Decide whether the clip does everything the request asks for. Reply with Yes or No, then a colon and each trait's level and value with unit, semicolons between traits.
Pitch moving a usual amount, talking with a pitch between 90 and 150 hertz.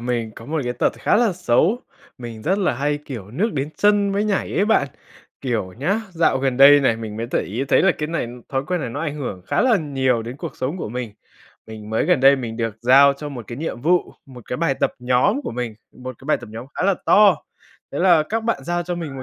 No: wide, 6.3 semitones; low, 135 Hz